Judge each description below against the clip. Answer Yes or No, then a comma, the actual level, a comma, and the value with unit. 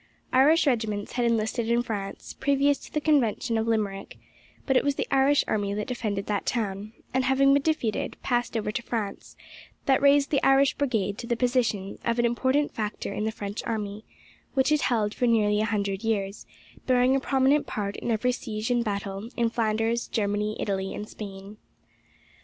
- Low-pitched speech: No, high, 230 Hz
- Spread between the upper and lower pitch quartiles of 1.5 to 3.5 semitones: No, average, 3.9 semitones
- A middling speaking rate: Yes, average, 185 wpm